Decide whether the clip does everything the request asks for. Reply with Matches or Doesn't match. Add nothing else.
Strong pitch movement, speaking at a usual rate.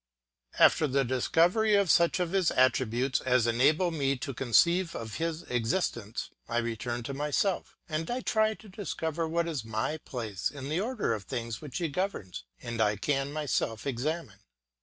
Matches